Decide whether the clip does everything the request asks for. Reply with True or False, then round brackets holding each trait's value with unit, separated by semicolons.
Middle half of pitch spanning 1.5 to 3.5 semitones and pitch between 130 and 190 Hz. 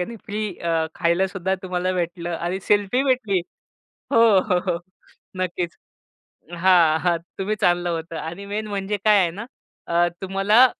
True (2.8 semitones; 185 Hz)